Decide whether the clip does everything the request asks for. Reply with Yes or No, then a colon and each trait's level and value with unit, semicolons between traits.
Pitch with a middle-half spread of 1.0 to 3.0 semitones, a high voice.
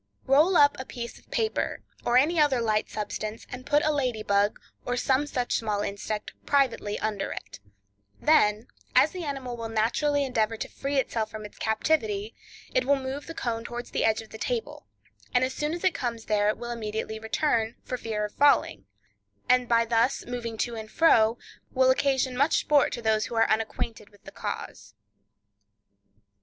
No: average, 4.0 semitones; high, 235 Hz